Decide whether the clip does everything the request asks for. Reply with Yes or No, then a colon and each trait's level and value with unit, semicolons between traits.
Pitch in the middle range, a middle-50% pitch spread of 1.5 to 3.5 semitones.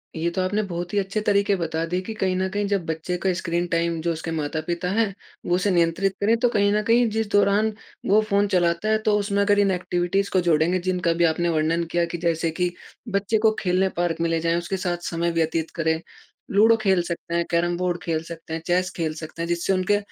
Yes: medium, 175 Hz; average, 3.0 semitones